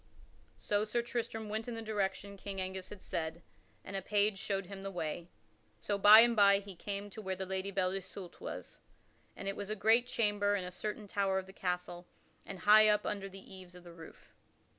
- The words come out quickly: Yes, fast, 215 wpm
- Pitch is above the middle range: Yes, high, 195 Hz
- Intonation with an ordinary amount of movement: No, narrow, 1.9 semitones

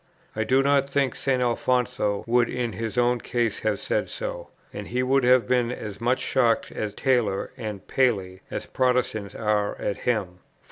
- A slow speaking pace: No, average, 175 wpm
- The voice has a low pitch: Yes, low, 120 Hz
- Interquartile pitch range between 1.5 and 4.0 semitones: Yes, average, 3.1 semitones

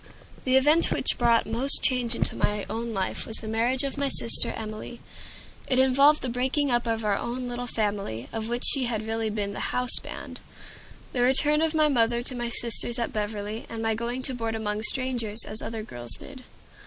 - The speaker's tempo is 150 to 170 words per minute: No, average, 200 wpm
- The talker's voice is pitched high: Yes, high, 235 Hz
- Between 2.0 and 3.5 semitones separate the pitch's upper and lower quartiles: Yes, average, 2.8 semitones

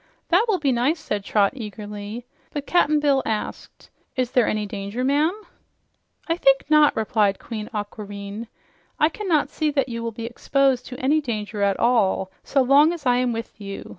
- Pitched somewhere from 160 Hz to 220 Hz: No, high, 245 Hz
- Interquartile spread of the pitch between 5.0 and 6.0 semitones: Yes, average, 5.3 semitones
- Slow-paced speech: No, average, 175 wpm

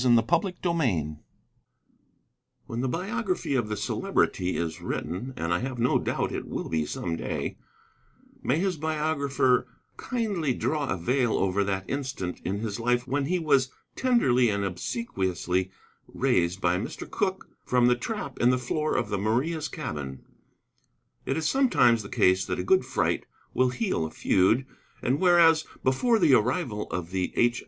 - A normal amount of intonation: No, wide, 8.3 semitones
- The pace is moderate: Yes, average, 160 wpm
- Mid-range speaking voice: No, low, 125 Hz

